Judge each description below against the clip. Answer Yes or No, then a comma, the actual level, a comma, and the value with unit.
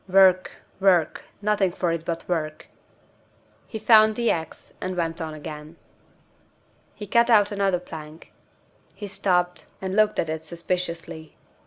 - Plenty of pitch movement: No, average, 3.4 semitones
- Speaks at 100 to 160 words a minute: Yes, average, 140 wpm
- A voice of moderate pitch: Yes, medium, 180 Hz